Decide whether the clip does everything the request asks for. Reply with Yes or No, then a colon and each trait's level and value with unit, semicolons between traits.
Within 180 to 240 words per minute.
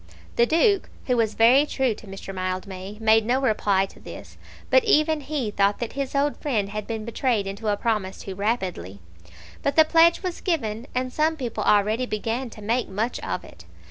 Yes: average, 195 wpm